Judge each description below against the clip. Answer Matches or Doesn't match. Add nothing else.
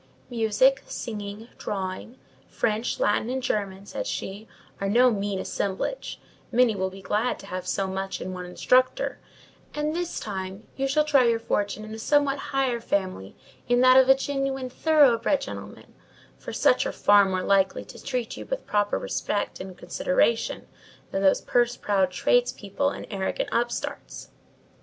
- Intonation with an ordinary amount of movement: Matches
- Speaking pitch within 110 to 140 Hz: Doesn't match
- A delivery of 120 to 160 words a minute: Matches